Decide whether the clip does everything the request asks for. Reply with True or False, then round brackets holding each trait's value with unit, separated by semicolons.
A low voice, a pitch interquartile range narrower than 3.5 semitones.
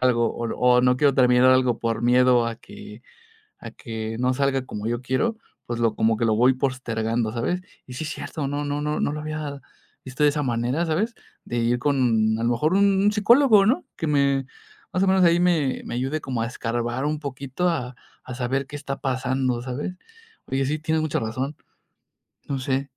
False (130 Hz; 3.8 semitones)